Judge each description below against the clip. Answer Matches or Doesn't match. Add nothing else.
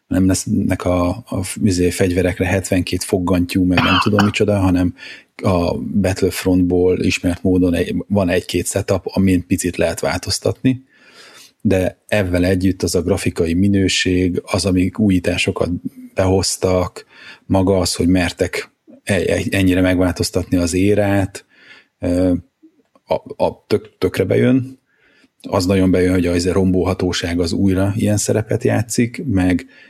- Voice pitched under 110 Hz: Matches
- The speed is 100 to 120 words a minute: Doesn't match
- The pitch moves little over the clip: Matches